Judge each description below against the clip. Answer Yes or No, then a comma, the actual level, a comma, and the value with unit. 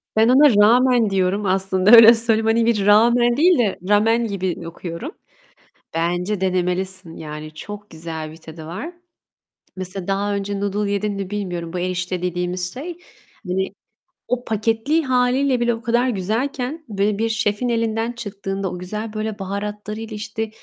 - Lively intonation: No, average, 3.7 semitones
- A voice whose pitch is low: No, high, 205 Hz